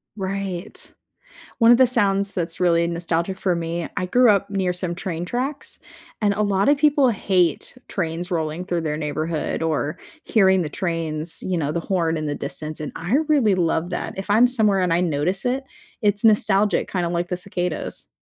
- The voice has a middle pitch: Yes, medium, 180 Hz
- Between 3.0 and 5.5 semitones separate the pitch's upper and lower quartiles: Yes, average, 3.5 semitones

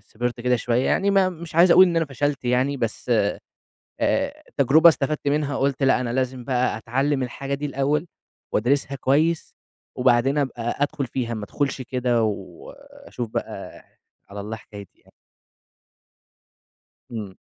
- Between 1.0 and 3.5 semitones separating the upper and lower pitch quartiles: Yes, average, 3.2 semitones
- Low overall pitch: Yes, low, 130 Hz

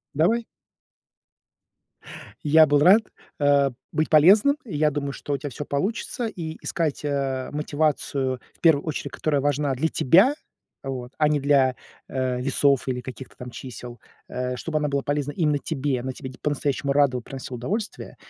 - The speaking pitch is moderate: Yes, medium, 145 Hz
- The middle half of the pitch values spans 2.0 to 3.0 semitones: Yes, average, 2.7 semitones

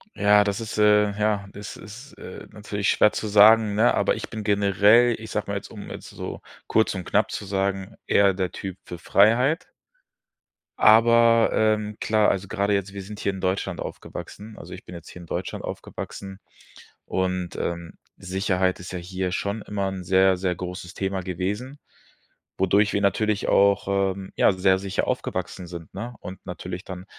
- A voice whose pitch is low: Yes, low, 100 Hz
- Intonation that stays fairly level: Yes, narrow, 2.1 semitones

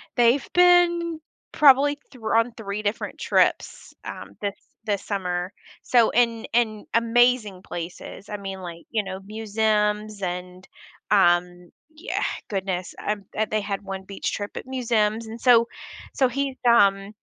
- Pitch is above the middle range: Yes, high, 215 Hz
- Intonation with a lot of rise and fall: No, average, 3.5 semitones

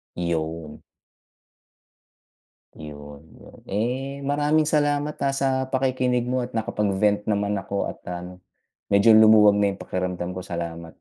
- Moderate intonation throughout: No, wide, 6.4 semitones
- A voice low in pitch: Yes, low, 105 Hz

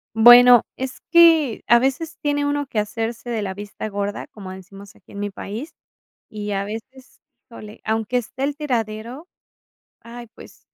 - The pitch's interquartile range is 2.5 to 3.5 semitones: No, average, 4.1 semitones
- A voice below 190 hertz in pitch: No, high, 230 Hz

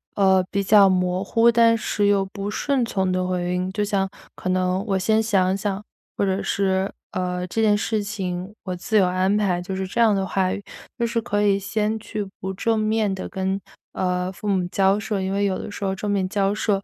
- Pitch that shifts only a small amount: Yes, narrow, 1.9 semitones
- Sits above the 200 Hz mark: No, high, 195 Hz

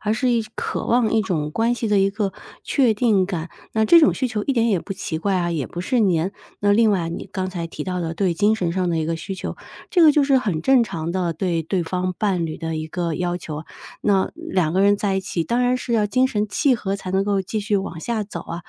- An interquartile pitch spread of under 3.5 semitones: No, average, 4.3 semitones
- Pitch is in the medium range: No, high, 195 Hz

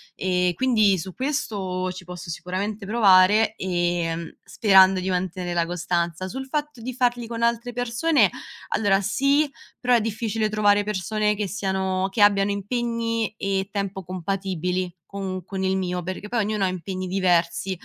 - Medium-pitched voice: No, high, 195 Hz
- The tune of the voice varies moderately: Yes, average, 3.2 semitones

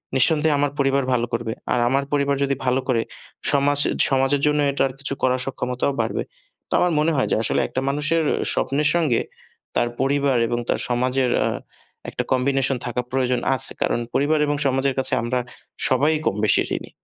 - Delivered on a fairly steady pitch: Yes, narrow, 2.1 semitones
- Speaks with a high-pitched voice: No, low, 135 Hz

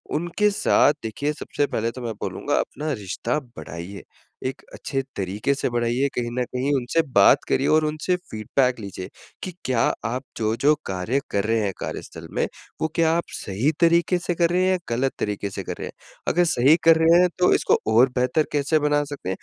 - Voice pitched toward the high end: No, low, 130 Hz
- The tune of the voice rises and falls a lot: Yes, wide, 5.9 semitones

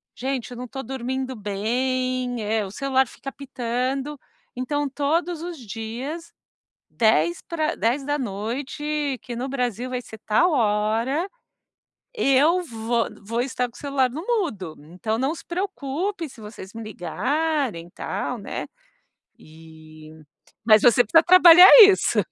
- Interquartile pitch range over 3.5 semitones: Yes, average, 4.9 semitones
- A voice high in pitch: Yes, very high, 255 Hz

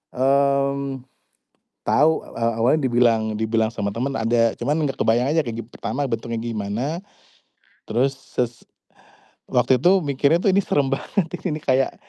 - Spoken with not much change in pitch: No, average, 3.3 semitones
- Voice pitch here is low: Yes, low, 130 Hz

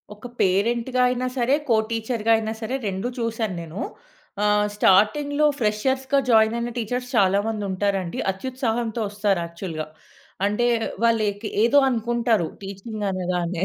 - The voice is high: Yes, high, 220 Hz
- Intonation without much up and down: No, average, 3.3 semitones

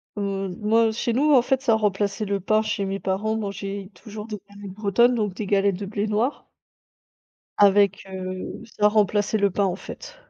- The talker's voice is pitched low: No, high, 205 Hz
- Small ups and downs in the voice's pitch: Yes, narrow, 1.8 semitones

